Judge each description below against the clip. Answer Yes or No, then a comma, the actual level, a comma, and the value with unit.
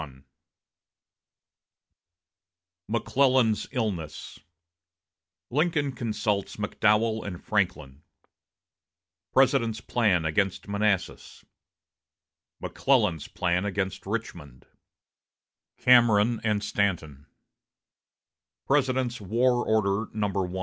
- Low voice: Yes, low, 105 Hz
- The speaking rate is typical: No, slow, 65 wpm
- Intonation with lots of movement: No, average, 3.8 semitones